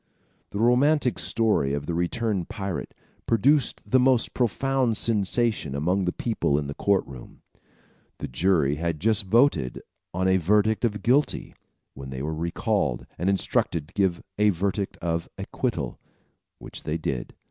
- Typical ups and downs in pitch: No, wide, 6.2 semitones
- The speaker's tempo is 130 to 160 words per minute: Yes, average, 155 wpm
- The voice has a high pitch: No, very low, 95 Hz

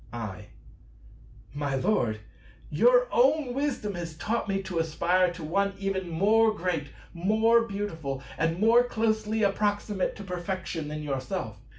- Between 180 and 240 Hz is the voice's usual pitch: Yes, high, 190 Hz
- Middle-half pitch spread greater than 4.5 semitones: Yes, average, 5.1 semitones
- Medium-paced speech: No, slow, 130 wpm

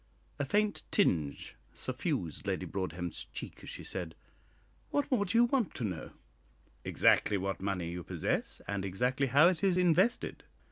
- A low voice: Yes, low, 125 Hz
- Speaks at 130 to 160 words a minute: Yes, average, 155 wpm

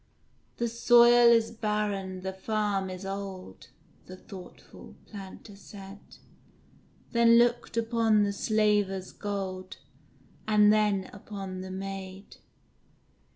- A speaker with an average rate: No, slow, 105 wpm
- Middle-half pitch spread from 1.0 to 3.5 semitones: Yes, narrow, 2.4 semitones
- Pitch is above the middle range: Yes, high, 205 Hz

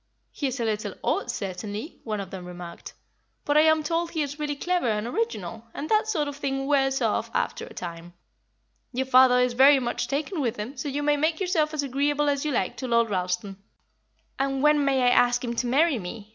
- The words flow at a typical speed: No, fast, 220 wpm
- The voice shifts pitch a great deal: No, average, 4.8 semitones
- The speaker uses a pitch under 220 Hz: No, very high, 270 Hz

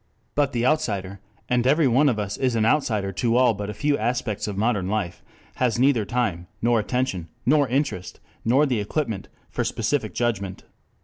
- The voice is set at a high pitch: No, low, 115 Hz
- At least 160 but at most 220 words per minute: Yes, average, 180 wpm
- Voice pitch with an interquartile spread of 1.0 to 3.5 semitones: No, average, 4.1 semitones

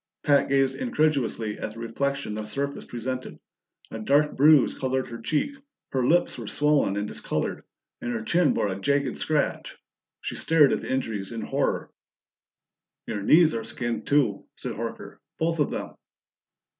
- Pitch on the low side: Yes, low, 130 Hz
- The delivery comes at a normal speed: Yes, average, 160 wpm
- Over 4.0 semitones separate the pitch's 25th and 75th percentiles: Yes, average, 4.7 semitones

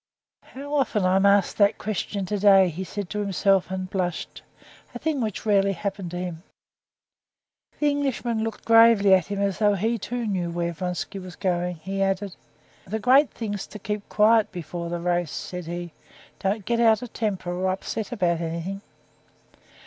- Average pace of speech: Yes, average, 180 wpm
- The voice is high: Yes, high, 195 Hz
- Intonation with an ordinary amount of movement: Yes, average, 3.3 semitones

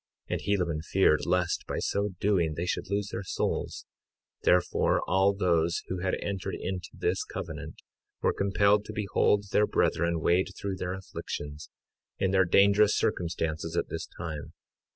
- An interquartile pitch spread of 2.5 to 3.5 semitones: Yes, average, 2.8 semitones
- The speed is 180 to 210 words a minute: No, average, 155 wpm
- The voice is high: No, very low, 95 Hz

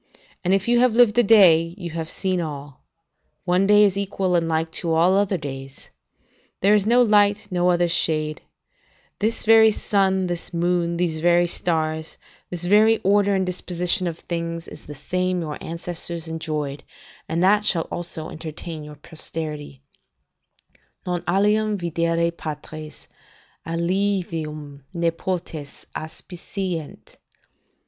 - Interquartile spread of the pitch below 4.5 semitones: Yes, average, 3.2 semitones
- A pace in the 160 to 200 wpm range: No, average, 140 wpm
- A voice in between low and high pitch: Yes, medium, 175 Hz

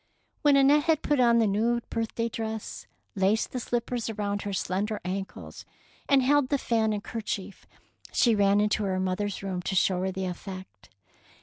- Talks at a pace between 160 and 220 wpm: Yes, average, 180 wpm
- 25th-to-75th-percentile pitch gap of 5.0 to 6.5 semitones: No, average, 3.5 semitones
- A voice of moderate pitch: No, high, 210 Hz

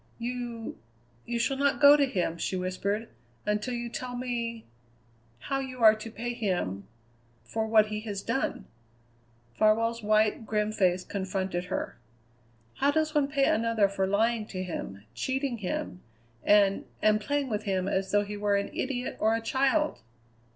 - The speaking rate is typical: Yes, average, 160 wpm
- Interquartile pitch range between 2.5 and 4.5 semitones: Yes, average, 3.7 semitones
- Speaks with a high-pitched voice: Yes, high, 220 Hz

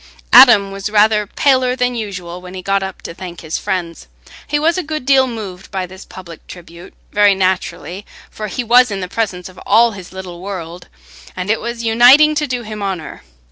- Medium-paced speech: Yes, average, 195 wpm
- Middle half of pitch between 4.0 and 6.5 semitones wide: Yes, average, 4.4 semitones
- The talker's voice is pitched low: No, high, 200 Hz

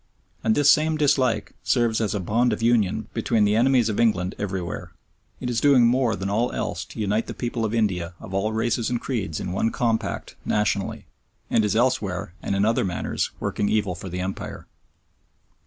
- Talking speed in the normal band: Yes, average, 190 wpm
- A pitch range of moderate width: Yes, average, 3.5 semitones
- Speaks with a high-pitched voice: No, low, 110 Hz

